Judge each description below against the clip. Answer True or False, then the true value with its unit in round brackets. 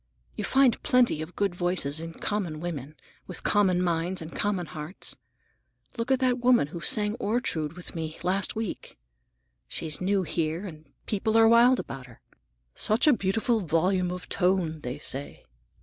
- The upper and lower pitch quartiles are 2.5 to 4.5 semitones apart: False (5.1 semitones)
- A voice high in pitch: False (180 Hz)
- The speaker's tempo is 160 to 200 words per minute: True (165 wpm)